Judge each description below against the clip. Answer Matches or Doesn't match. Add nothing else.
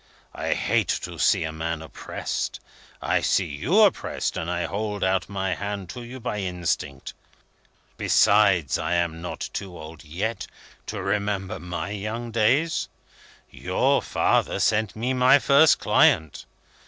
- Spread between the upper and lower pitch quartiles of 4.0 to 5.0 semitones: Matches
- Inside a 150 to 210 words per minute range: Doesn't match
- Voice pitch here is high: Doesn't match